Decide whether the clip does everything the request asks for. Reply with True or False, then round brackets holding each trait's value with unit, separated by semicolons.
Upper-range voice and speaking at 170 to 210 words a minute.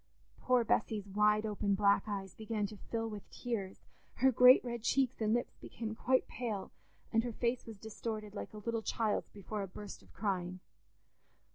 True (215 Hz; 180 wpm)